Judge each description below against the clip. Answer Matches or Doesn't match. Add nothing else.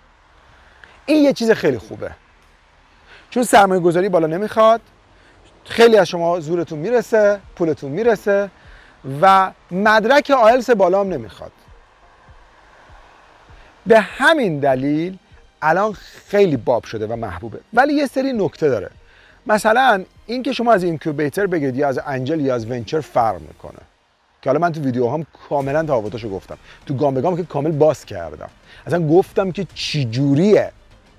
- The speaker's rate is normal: Matches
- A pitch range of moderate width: Doesn't match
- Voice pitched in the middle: Matches